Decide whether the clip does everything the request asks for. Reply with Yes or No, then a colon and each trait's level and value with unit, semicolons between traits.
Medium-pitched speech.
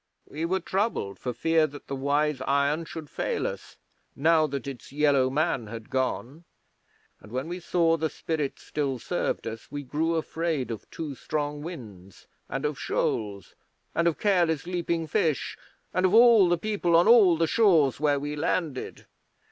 Yes: medium, 150 Hz